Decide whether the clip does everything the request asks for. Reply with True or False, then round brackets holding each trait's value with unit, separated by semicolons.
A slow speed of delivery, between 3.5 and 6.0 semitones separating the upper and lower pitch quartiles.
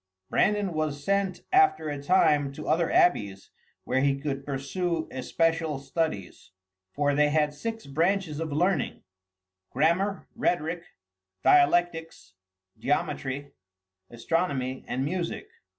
True (110 wpm; 3.8 semitones)